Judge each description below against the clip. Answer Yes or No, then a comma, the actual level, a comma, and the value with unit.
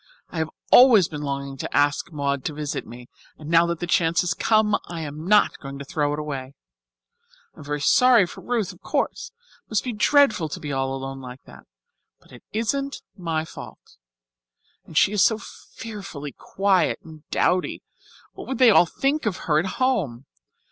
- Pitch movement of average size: No, wide, 6.6 semitones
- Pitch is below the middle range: No, medium, 165 Hz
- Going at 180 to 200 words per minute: Yes, average, 190 wpm